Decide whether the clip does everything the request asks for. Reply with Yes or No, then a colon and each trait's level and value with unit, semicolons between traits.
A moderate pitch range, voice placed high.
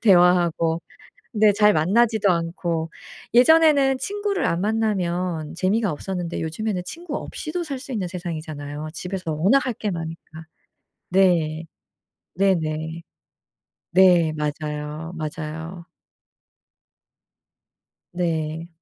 No: average, 4.7 semitones; medium, 175 Hz